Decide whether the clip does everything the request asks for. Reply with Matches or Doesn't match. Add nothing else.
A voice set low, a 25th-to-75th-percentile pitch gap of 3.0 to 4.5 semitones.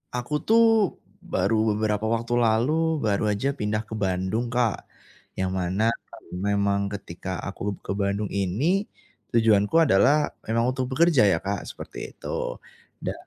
Matches